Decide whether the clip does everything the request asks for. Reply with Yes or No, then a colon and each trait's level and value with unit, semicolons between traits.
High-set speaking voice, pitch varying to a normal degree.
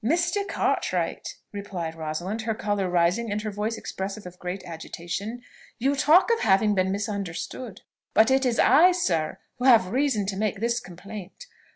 Yes: high, 210 Hz; average, 4.7 semitones